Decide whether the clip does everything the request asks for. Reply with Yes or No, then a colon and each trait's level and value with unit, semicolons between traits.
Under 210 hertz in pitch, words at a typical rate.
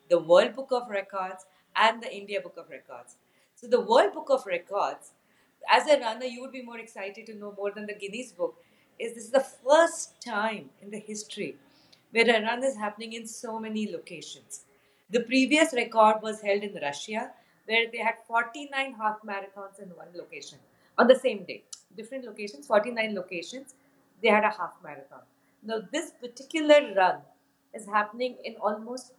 No: high, 225 Hz; average, 180 wpm